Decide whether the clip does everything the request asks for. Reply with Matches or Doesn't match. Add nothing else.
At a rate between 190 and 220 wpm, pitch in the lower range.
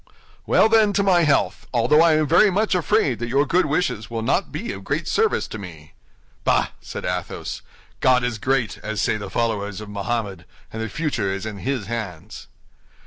Matches